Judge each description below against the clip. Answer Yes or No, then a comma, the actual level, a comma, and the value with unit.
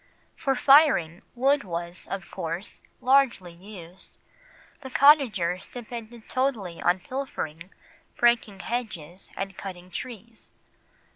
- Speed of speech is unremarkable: No, slow, 100 wpm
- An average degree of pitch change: No, wide, 6.3 semitones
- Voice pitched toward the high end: Yes, high, 210 Hz